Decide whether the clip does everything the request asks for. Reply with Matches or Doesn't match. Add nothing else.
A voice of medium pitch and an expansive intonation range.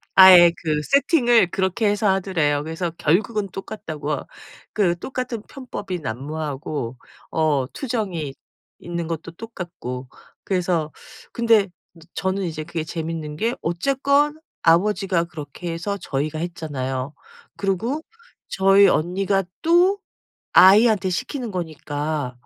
Doesn't match